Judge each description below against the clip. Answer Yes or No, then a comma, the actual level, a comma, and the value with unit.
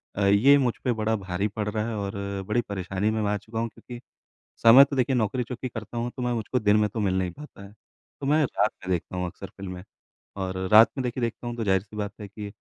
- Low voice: Yes, low, 105 Hz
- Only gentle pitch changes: No, average, 3.2 semitones